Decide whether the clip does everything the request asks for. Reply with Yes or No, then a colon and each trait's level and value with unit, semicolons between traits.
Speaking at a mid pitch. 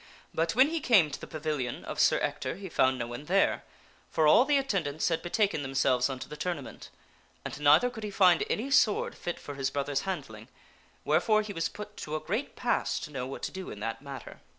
Yes: medium, 155 Hz